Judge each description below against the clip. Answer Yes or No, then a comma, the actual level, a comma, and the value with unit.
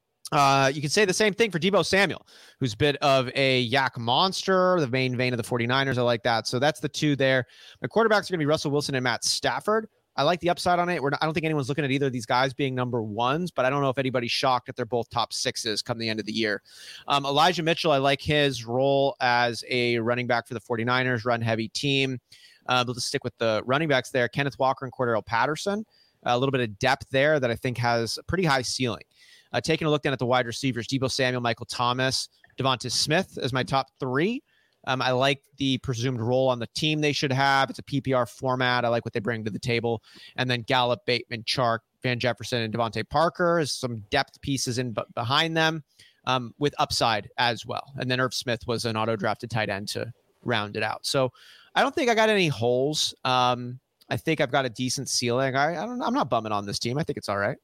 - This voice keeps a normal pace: No, fast, 245 wpm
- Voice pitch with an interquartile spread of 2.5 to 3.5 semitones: Yes, average, 3.0 semitones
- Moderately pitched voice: No, low, 130 Hz